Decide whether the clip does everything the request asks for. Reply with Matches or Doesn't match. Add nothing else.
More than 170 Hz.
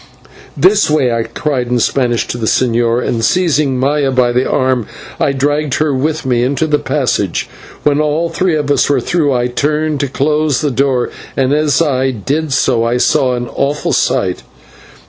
Doesn't match